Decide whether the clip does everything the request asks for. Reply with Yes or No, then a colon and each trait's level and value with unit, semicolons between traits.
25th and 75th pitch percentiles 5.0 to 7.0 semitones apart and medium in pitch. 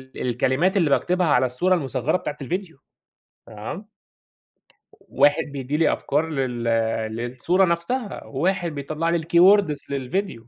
Yes: wide, 5.4 semitones; medium, 155 Hz